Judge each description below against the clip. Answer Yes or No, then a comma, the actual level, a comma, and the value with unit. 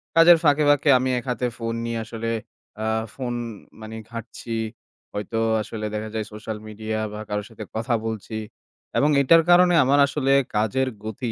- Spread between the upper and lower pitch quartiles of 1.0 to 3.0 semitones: No, average, 3.8 semitones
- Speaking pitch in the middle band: No, low, 115 Hz